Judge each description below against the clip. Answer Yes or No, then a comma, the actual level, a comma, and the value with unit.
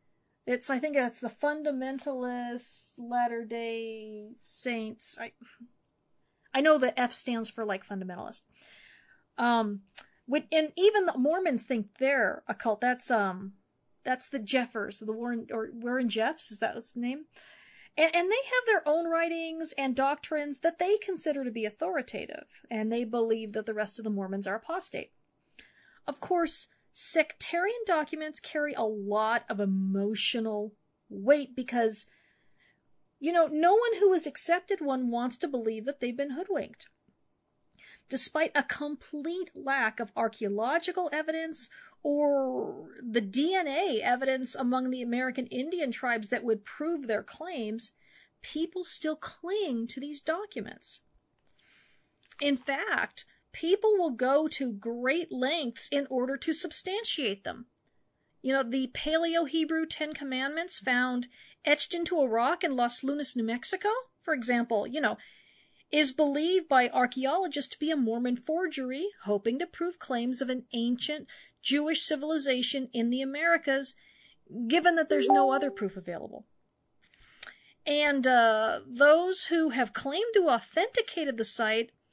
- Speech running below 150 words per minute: Yes, average, 140 wpm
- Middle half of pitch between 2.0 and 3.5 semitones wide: No, average, 5.2 semitones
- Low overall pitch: No, very high, 270 Hz